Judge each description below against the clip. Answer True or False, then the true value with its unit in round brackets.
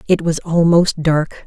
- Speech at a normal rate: True (165 wpm)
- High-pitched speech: False (165 Hz)